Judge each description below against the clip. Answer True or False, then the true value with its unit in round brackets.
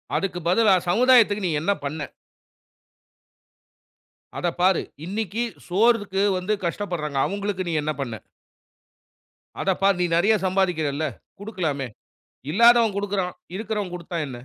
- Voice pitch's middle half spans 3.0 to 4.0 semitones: True (3.3 semitones)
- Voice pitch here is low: False (190 Hz)